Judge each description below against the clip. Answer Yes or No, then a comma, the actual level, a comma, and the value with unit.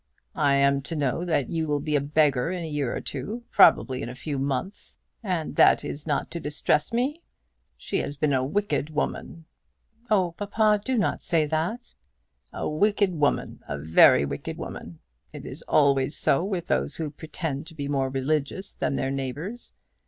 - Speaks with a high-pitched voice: No, medium, 150 Hz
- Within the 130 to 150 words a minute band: No, average, 180 wpm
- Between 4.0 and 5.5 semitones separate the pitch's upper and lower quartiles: Yes, average, 4.3 semitones